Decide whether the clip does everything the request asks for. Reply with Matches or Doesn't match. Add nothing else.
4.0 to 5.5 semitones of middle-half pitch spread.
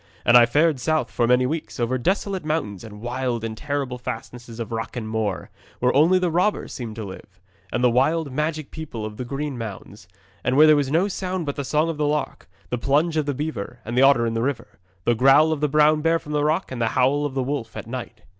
Matches